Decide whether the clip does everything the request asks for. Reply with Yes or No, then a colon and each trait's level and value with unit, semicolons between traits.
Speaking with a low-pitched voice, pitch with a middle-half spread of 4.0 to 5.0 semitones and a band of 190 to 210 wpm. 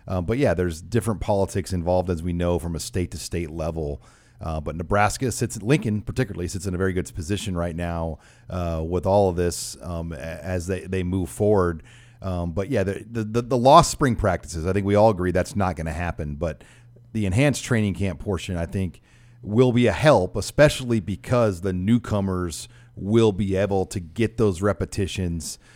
Yes: very low, 95 Hz; average, 4.3 semitones; average, 195 wpm